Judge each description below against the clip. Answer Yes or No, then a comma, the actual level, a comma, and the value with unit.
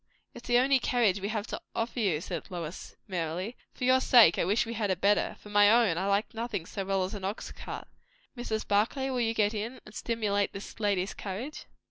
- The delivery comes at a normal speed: No, fast, 220 wpm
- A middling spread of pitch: Yes, average, 3.2 semitones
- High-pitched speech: Yes, high, 210 Hz